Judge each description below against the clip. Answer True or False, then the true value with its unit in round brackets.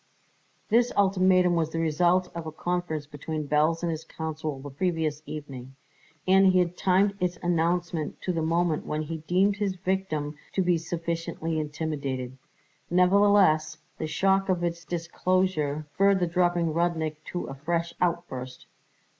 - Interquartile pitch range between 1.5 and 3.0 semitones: True (2.7 semitones)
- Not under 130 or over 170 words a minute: True (150 wpm)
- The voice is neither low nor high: True (170 Hz)